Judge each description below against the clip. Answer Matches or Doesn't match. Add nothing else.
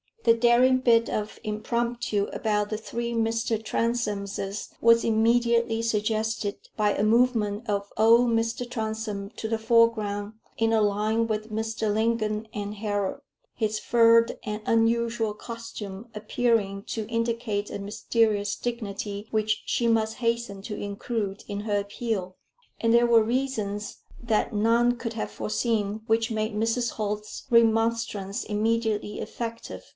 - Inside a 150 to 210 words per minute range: Doesn't match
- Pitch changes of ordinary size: Doesn't match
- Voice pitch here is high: Matches